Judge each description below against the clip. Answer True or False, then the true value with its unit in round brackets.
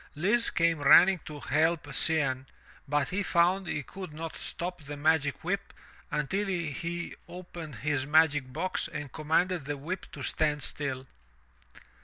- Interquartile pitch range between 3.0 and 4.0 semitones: True (3.4 semitones)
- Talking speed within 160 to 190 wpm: False (150 wpm)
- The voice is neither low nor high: True (160 Hz)